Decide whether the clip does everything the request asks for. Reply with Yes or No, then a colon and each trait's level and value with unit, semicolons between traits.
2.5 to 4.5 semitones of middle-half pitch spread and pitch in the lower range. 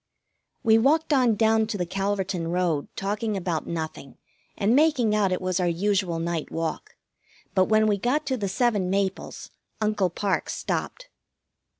No: average, 3.6 semitones; high, 200 Hz